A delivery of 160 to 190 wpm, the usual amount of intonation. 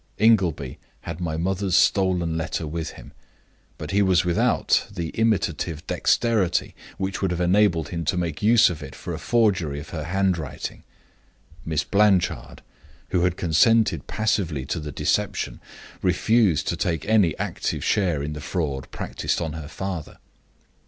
No: average, 150 wpm; average, 3.6 semitones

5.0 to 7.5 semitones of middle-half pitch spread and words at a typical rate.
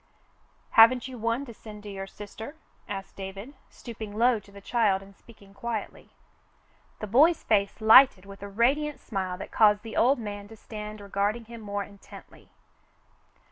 No: average, 2.8 semitones; average, 170 wpm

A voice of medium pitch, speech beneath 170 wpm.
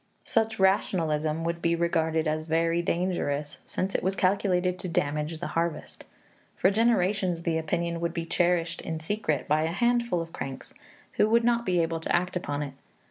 No: medium, 170 Hz; average, 180 wpm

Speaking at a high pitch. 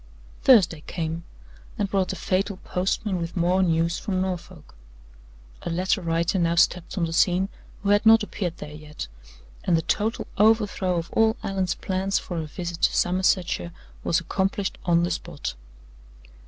No: medium, 180 Hz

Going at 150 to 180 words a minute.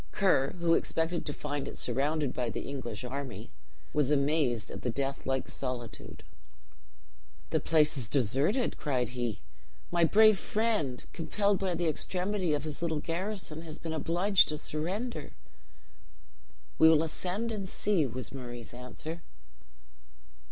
No: average, 140 wpm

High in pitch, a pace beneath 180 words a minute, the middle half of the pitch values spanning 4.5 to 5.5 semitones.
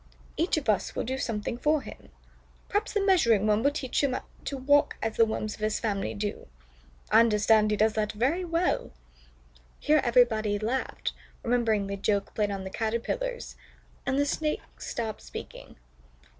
Yes: high, 230 Hz; average, 170 wpm; average, 5.1 semitones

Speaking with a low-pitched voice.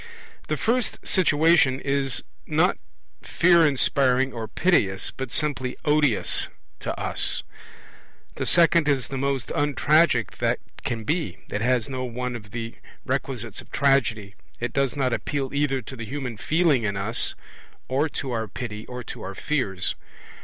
Yes: low, 130 Hz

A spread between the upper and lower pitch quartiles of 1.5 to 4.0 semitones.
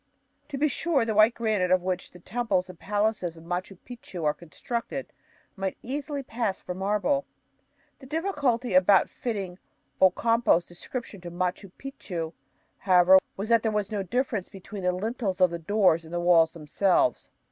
No: average, 4.6 semitones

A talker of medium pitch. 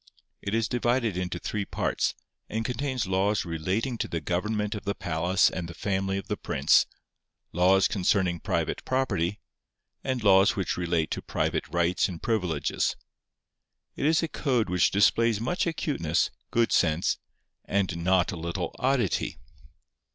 No: low, 100 Hz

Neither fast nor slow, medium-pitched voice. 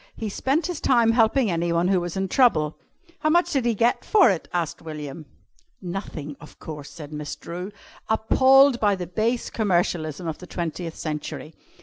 Yes: average, 175 wpm; medium, 180 Hz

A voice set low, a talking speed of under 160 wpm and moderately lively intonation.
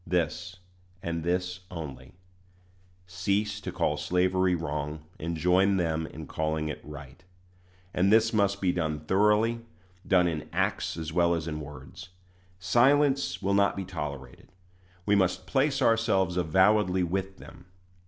Yes: very low, 90 Hz; average, 140 wpm; average, 3.7 semitones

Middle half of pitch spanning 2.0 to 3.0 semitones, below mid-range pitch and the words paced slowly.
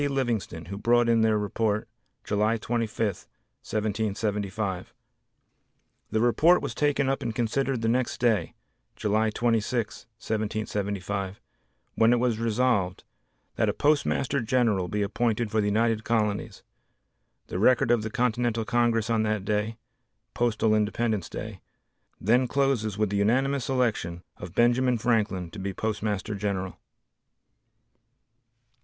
Yes: narrow, 2.6 semitones; low, 110 Hz; slow, 125 wpm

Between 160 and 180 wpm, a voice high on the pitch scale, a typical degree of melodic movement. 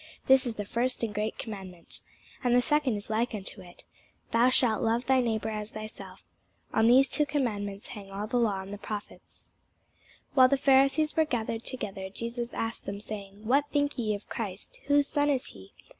No: average, 190 wpm; high, 225 Hz; average, 4.0 semitones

